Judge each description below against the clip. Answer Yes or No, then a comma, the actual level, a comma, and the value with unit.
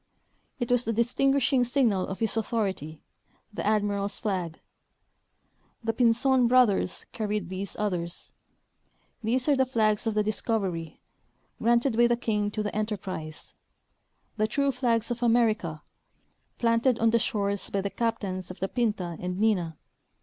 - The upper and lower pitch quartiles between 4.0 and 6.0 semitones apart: No, average, 3.4 semitones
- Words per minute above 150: No, average, 145 wpm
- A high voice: Yes, high, 215 Hz